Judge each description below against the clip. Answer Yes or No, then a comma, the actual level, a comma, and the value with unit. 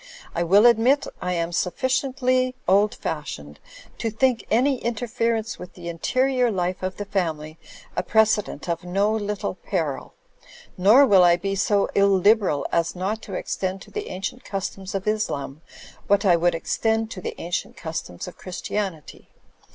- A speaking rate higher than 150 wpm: Yes, average, 160 wpm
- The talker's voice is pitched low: No, high, 195 Hz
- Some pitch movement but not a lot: Yes, average, 4.1 semitones